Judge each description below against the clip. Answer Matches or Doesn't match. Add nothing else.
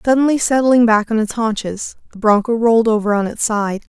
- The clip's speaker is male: Doesn't match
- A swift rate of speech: Doesn't match